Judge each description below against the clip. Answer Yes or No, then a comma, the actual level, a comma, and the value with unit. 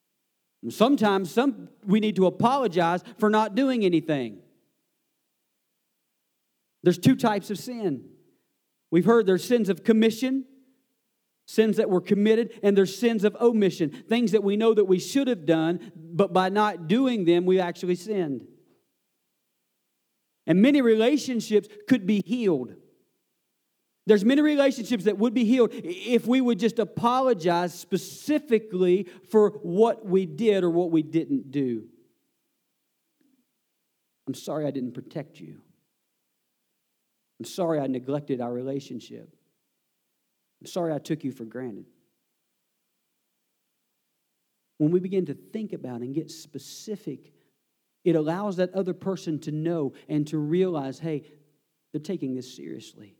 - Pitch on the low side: No, high, 190 Hz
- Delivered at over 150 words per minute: No, slow, 135 wpm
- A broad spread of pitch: Yes, wide, 5.8 semitones